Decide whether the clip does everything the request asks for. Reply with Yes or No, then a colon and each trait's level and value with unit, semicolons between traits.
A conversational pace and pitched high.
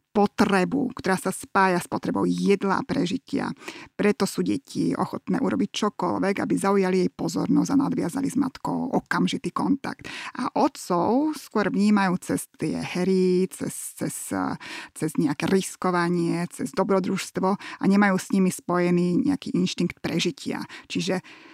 Yes: average, 135 wpm; high, 195 Hz